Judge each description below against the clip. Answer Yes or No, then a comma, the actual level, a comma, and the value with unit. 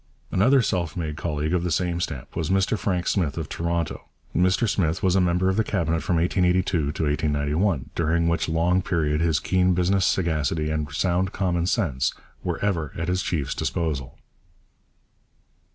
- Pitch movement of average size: Yes, average, 3.0 semitones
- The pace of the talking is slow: No, average, 170 wpm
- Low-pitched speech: Yes, very low, 85 Hz